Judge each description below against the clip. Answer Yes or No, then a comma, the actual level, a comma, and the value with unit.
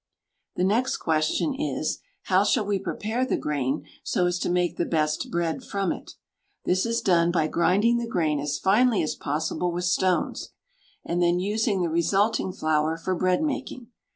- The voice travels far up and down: No, average, 4.1 semitones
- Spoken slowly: No, average, 175 wpm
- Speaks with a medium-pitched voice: Yes, medium, 180 Hz